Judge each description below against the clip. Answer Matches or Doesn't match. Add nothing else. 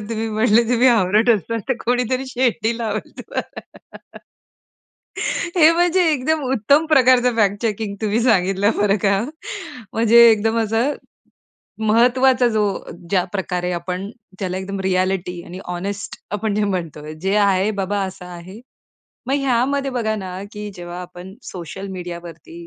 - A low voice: Doesn't match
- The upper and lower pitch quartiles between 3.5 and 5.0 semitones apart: Matches